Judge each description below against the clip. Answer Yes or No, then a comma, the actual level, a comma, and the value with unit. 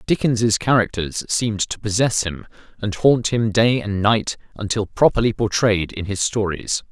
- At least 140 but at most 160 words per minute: Yes, average, 155 wpm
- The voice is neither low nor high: No, low, 110 Hz